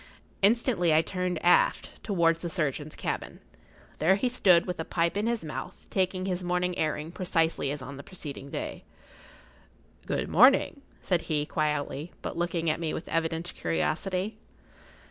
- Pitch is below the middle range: No, medium, 170 Hz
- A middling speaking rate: Yes, average, 155 wpm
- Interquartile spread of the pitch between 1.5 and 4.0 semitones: Yes, average, 3.0 semitones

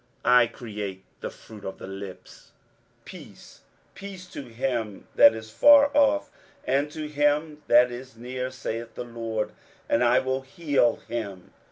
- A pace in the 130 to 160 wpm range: Yes, average, 155 wpm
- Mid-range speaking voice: No, low, 125 Hz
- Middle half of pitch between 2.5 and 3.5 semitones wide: No, average, 4.7 semitones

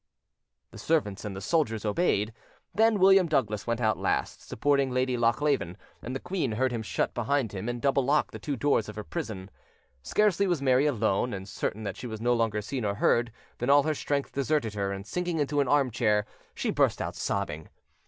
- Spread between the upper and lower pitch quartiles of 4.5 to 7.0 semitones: Yes, wide, 5.4 semitones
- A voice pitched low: Yes, low, 125 Hz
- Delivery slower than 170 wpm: No, fast, 205 wpm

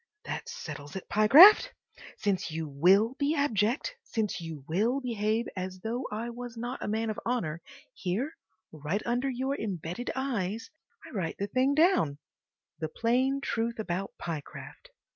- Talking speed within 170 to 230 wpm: No, average, 145 wpm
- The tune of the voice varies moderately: No, wide, 5.7 semitones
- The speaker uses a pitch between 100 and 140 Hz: No, high, 220 Hz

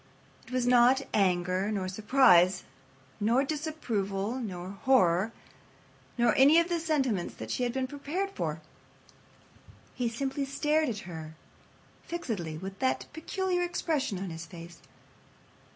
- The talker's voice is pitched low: No, high, 235 Hz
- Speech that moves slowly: Yes, slow, 130 wpm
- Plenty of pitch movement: Yes, wide, 7.2 semitones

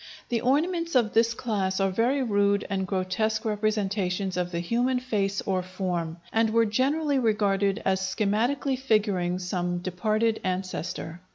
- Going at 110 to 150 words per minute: Yes, average, 145 wpm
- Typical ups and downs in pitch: Yes, average, 3.7 semitones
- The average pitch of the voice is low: No, high, 205 Hz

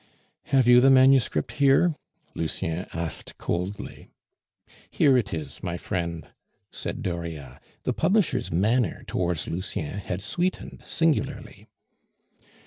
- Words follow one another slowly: Yes, slow, 110 wpm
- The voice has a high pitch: No, very low, 95 Hz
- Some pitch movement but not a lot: No, wide, 7.8 semitones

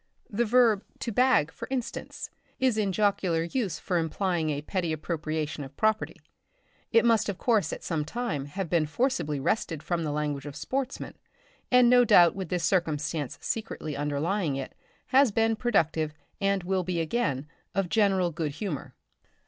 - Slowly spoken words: No, average, 165 wpm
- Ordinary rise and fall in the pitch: No, wide, 6.4 semitones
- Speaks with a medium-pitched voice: Yes, medium, 180 Hz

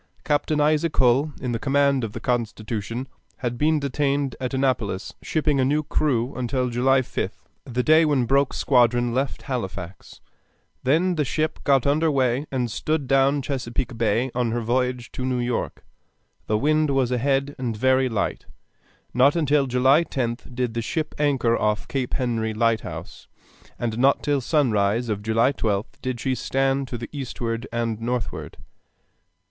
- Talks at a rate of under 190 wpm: Yes, average, 160 wpm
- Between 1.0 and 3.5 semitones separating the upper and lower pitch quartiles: Yes, average, 3.0 semitones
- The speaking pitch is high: No, low, 130 Hz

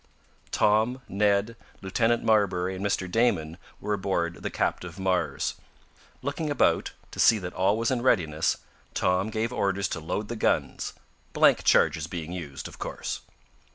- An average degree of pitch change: Yes, average, 3.8 semitones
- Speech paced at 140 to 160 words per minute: Yes, average, 150 wpm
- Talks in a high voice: No, low, 100 Hz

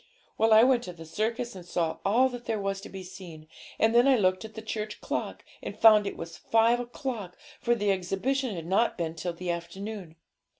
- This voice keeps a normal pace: No, fast, 215 wpm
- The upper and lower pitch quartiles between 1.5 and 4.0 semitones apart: No, average, 4.5 semitones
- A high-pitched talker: Yes, high, 205 Hz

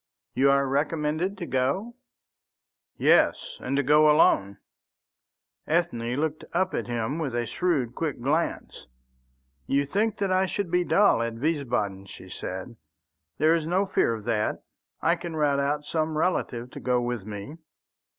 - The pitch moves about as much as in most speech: No, wide, 5.7 semitones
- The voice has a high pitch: No, medium, 145 Hz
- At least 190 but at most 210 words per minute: No, average, 155 wpm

